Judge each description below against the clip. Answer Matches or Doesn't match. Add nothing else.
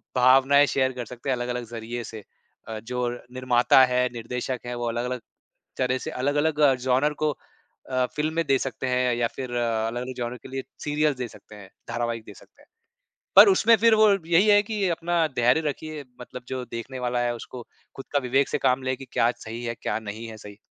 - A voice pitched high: Doesn't match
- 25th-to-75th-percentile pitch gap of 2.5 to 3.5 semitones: Matches